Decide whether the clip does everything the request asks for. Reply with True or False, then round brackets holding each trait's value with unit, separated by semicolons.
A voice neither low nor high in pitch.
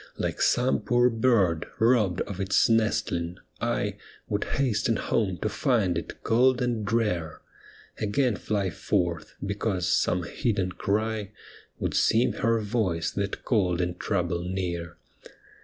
False (105 Hz)